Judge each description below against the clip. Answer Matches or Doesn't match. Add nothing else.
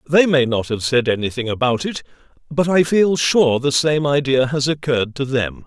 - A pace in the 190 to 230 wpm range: Matches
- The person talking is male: Matches